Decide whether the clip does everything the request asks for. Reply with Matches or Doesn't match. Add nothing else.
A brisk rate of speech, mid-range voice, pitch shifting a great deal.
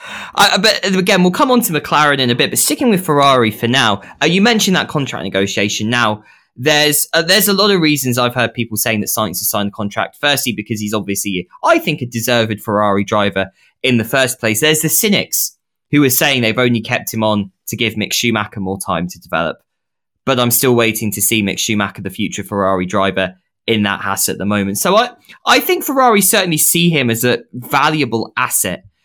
Doesn't match